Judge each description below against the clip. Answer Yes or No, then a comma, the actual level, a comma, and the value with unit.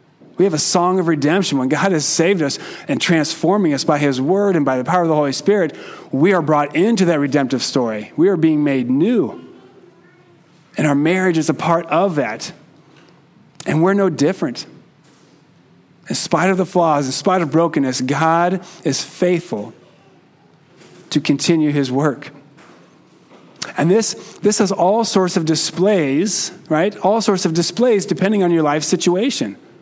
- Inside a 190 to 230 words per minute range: No, average, 165 wpm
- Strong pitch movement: No, average, 3.7 semitones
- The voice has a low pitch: No, medium, 170 Hz